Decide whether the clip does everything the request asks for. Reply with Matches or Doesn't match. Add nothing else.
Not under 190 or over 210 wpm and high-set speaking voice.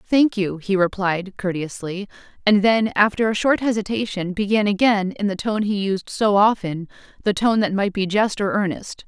Doesn't match